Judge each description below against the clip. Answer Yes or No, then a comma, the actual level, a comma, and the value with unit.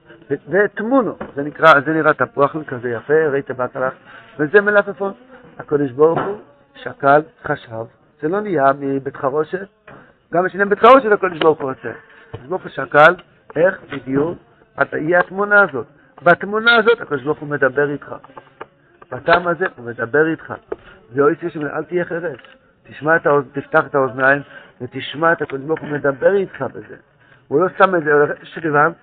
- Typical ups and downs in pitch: Yes, average, 4.3 semitones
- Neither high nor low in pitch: Yes, medium, 155 Hz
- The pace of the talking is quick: Yes, fast, 155 wpm